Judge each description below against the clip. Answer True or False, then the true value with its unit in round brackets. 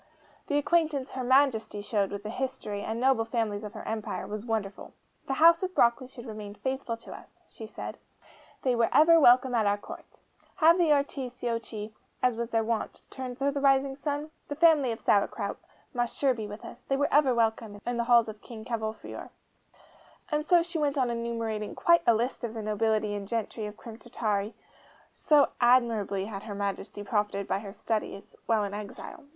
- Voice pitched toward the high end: True (235 Hz)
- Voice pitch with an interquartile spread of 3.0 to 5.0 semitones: True (4.0 semitones)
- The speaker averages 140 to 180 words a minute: False (190 wpm)